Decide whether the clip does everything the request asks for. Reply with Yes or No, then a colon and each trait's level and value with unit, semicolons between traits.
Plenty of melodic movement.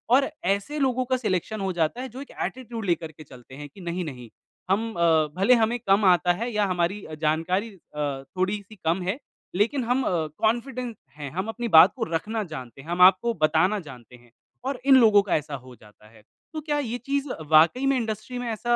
Yes: wide, 7.1 semitones